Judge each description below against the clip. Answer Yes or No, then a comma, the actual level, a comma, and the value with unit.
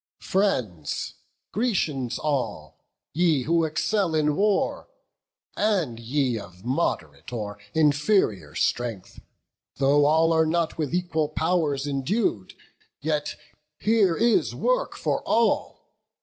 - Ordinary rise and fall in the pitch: No, wide, 6.0 semitones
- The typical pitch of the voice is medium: Yes, medium, 155 Hz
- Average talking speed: No, slow, 105 wpm